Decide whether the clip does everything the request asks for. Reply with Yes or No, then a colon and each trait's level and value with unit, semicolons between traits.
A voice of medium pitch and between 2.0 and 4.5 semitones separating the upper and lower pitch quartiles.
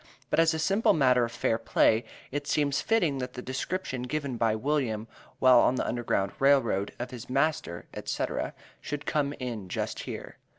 No: low, 130 Hz; average, 3.8 semitones